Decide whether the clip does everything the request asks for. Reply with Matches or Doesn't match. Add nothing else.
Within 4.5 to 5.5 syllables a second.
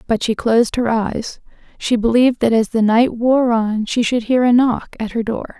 Matches